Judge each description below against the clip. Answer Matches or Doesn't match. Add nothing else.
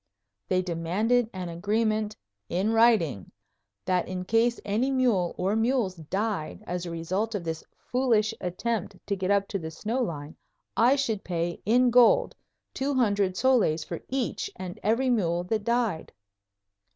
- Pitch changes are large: Doesn't match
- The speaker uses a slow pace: Doesn't match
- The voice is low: Doesn't match